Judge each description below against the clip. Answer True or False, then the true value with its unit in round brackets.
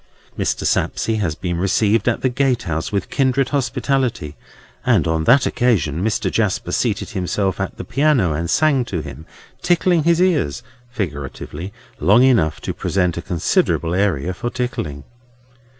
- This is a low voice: True (105 Hz)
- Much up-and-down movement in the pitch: True (7.2 semitones)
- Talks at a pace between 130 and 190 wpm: True (140 wpm)